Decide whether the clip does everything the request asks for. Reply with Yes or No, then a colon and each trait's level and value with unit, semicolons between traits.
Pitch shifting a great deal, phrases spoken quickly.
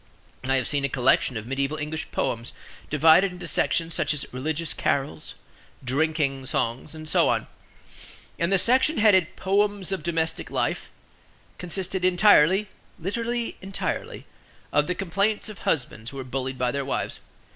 No: wide, 5.9 semitones; average, 150 wpm